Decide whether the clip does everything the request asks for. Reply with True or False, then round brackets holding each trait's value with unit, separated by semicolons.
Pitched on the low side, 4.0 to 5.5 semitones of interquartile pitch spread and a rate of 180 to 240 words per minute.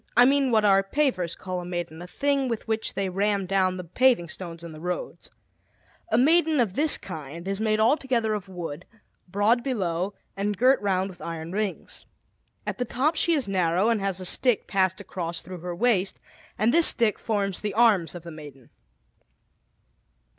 False (195 Hz; 4.9 semitones; 185 wpm)